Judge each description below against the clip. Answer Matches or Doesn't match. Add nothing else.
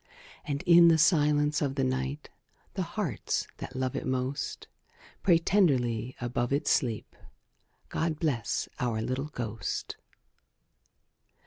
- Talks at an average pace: Doesn't match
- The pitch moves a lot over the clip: Doesn't match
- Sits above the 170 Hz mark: Doesn't match